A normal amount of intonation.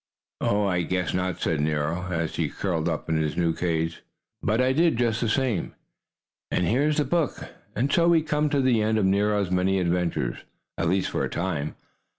No: wide, 6.4 semitones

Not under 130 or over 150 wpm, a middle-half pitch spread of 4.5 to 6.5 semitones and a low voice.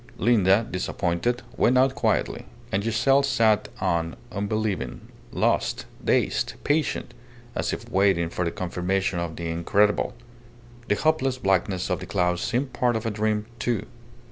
Yes: average, 145 wpm; average, 5.1 semitones; low, 105 Hz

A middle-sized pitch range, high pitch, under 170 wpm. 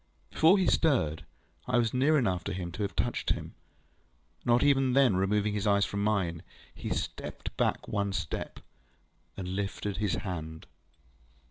No: average, 5.0 semitones; low, 105 Hz; average, 155 wpm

